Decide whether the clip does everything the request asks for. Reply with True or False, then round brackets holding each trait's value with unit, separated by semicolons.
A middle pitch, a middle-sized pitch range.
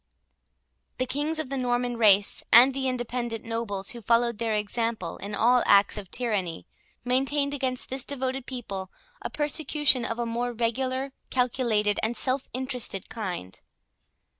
False (240 Hz; 3.1 semitones)